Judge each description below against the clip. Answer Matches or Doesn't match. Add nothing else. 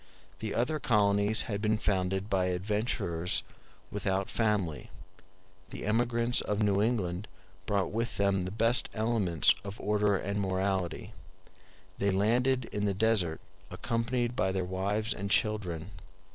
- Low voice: Matches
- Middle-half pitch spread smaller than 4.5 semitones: Matches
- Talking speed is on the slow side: Matches